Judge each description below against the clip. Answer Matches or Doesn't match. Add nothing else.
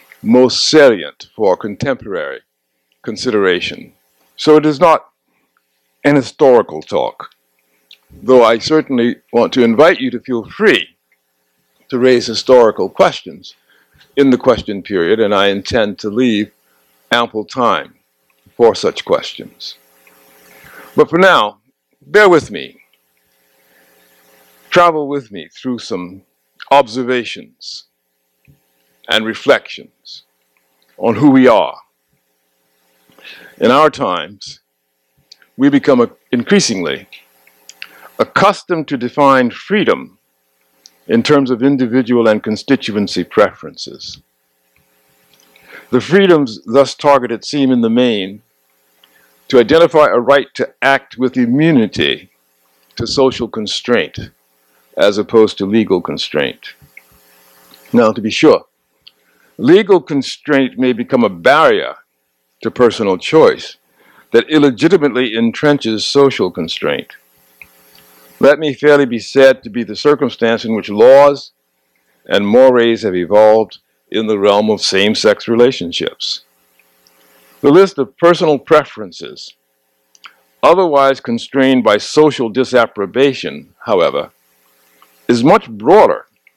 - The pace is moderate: Doesn't match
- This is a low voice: Matches